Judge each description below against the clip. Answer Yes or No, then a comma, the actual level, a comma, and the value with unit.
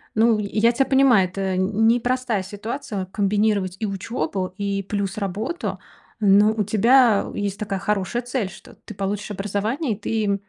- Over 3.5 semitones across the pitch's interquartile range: No, narrow, 2.6 semitones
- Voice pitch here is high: Yes, high, 210 Hz